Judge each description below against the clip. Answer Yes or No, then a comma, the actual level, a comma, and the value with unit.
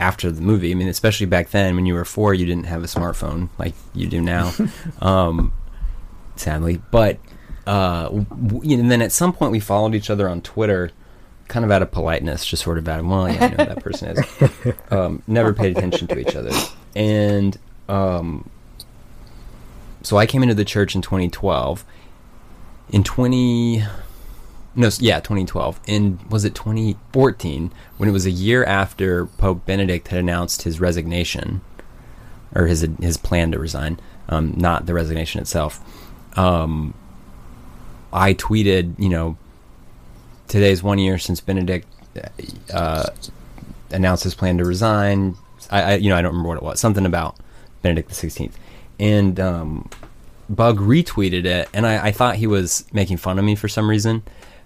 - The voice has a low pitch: Yes, very low, 95 Hz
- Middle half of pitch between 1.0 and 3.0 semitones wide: No, average, 3.6 semitones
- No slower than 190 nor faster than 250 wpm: No, average, 170 wpm